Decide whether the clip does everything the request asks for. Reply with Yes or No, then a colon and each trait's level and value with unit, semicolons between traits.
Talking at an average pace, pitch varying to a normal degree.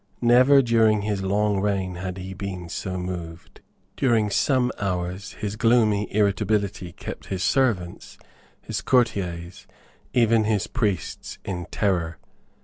No: slow, 125 wpm; average, 3.3 semitones